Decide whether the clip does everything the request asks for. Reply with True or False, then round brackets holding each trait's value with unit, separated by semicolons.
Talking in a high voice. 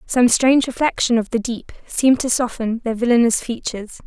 True (240 Hz)